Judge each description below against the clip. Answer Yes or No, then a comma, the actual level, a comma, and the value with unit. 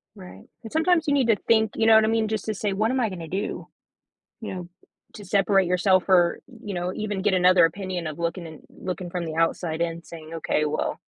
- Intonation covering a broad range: No, average, 4.2 semitones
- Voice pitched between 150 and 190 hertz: Yes, medium, 185 Hz